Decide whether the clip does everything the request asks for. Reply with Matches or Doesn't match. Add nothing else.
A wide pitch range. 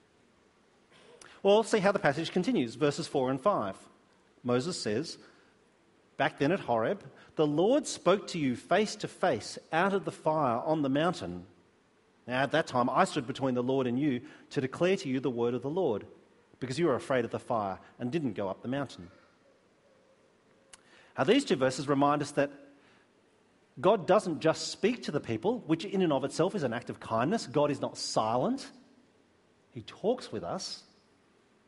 Matches